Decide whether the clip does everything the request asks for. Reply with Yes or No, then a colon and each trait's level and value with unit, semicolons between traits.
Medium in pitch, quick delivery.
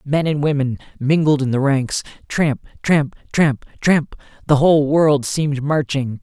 No: medium, 145 Hz; average, 155 wpm